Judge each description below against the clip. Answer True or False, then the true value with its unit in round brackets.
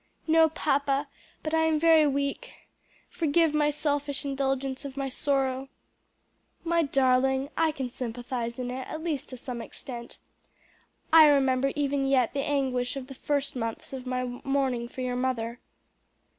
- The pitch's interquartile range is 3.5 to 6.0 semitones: False (2.4 semitones)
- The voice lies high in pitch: True (275 Hz)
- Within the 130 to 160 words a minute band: True (155 wpm)